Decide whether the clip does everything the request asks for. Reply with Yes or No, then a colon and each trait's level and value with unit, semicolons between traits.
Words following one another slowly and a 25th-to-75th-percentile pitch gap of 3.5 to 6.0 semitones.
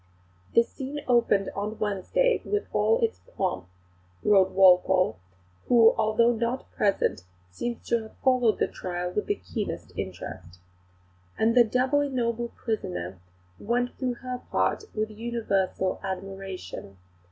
Yes: slow, 130 wpm; average, 4.5 semitones